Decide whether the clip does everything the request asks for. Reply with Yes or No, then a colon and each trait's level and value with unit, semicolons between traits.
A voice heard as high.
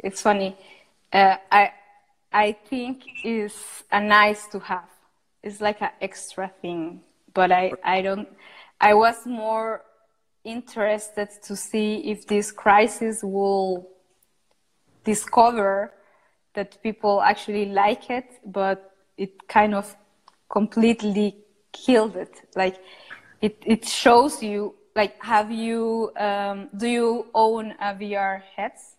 Yes: high, 210 Hz